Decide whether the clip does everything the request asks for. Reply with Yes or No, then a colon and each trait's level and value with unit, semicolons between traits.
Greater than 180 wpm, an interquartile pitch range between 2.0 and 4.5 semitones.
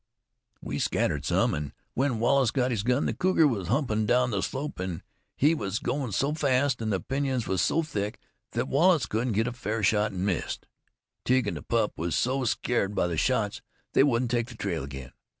No: fast, 205 wpm; average, 4.9 semitones